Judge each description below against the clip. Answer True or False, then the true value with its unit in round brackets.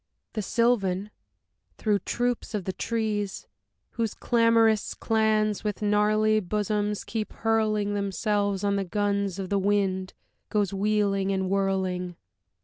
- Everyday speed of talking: False (125 wpm)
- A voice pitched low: False (205 Hz)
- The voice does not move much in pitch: True (1.6 semitones)